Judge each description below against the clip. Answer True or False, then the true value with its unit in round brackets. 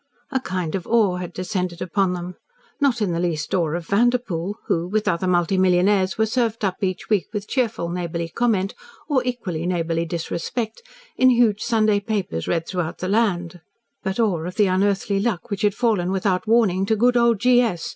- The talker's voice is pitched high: True (195 Hz)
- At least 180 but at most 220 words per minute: True (190 wpm)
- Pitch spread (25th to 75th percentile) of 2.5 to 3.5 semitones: False (4.0 semitones)